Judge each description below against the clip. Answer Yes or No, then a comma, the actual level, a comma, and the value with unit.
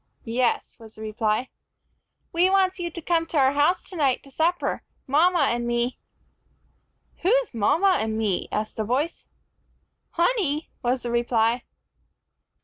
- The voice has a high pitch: Yes, very high, 270 Hz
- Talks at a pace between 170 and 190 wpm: No, average, 140 wpm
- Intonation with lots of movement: Yes, wide, 6.6 semitones